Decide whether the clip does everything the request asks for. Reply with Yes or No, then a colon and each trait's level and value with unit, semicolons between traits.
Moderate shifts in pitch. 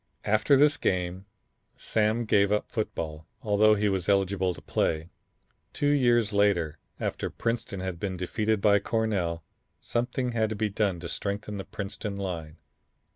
Yes: average, 3.0 semitones